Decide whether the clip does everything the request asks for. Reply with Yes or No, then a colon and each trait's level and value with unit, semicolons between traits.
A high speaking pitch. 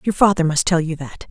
No: medium, 170 Hz